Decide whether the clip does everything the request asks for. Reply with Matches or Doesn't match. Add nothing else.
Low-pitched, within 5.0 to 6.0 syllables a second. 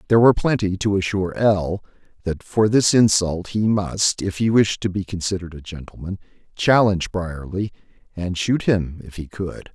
Matches